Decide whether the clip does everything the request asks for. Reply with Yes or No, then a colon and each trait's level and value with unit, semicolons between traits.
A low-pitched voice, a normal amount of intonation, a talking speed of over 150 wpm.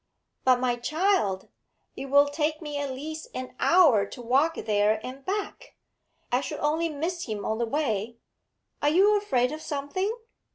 No: very high, 285 Hz; average, 4.6 semitones; average, 165 wpm